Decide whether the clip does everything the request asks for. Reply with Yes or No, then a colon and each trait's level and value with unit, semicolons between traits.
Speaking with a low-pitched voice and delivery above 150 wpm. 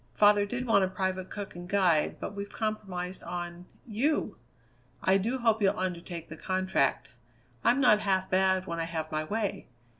No: high, 190 Hz; average, 175 wpm